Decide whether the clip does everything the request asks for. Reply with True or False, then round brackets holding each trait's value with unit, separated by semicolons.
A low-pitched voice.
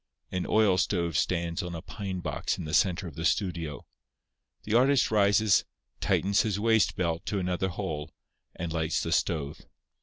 True (90 Hz)